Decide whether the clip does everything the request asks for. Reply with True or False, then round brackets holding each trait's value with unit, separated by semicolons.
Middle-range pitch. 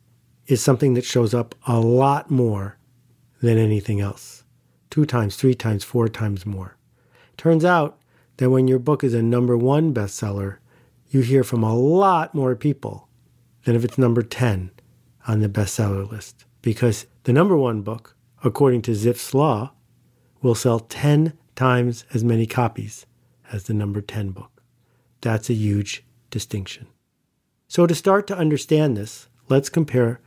False (120 Hz)